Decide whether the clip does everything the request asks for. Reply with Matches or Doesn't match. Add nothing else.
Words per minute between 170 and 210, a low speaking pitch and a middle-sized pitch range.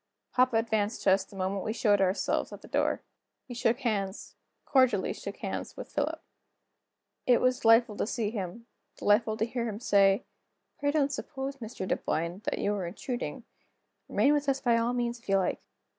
Doesn't match